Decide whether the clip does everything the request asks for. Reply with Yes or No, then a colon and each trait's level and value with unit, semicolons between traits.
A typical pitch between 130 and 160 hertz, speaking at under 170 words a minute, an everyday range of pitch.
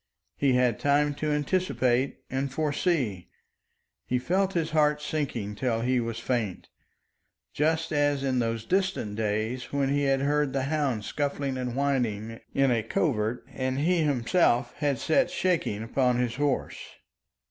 Yes: low, 135 Hz; average, 145 wpm; average, 3.7 semitones